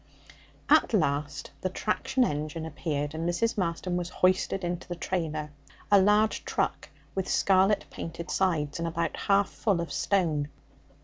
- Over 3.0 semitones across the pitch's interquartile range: Yes, average, 3.5 semitones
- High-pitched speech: No, medium, 175 Hz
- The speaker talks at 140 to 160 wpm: Yes, average, 145 wpm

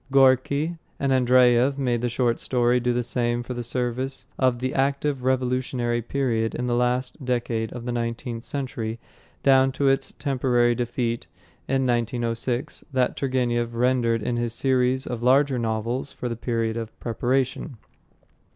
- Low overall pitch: Yes, low, 125 Hz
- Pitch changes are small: Yes, narrow, 1.7 semitones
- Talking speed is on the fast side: No, average, 145 wpm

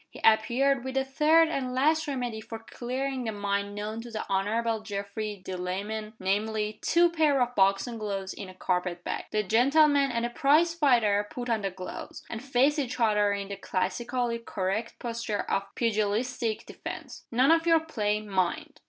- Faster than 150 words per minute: Yes, average, 175 wpm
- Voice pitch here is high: Yes, high, 225 Hz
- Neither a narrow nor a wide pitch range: Yes, average, 4.3 semitones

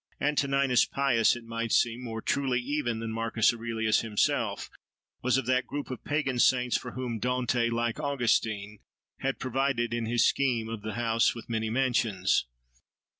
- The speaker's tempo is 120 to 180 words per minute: Yes, average, 160 wpm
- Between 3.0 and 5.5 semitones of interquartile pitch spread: No, narrow, 2.4 semitones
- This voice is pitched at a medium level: No, low, 120 Hz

